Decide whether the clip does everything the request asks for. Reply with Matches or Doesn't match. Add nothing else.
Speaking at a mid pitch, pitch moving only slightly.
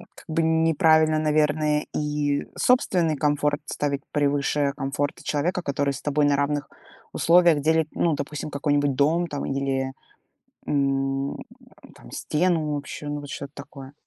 Matches